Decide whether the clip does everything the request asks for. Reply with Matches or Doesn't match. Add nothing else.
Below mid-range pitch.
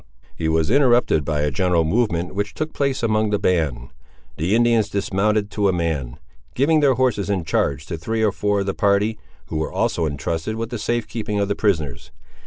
Matches